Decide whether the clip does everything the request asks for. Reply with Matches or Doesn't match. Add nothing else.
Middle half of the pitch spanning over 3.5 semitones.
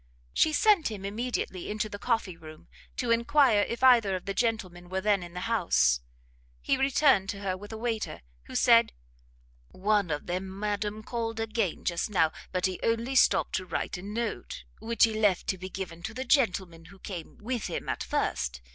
Matches